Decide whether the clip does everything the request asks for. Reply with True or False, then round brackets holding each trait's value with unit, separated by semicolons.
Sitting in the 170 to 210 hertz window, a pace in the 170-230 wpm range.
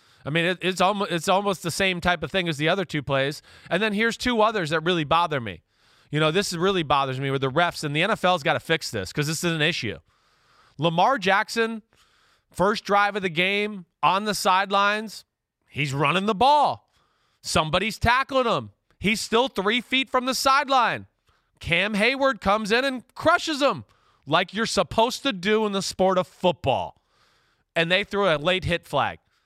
True (185 Hz; 185 wpm)